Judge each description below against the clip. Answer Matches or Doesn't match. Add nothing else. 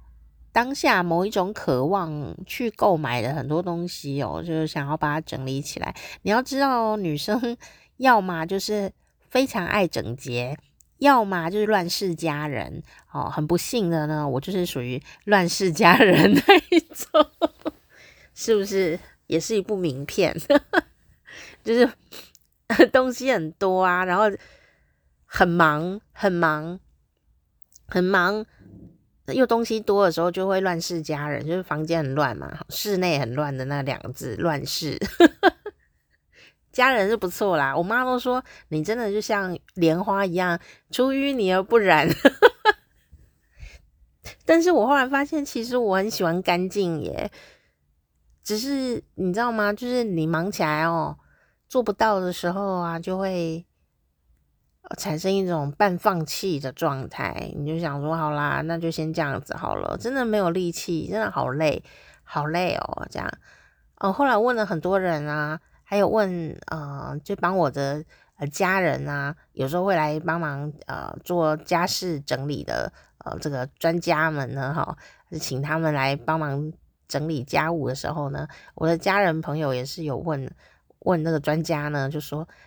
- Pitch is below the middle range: Doesn't match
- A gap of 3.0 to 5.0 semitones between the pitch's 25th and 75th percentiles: Doesn't match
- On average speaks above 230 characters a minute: Doesn't match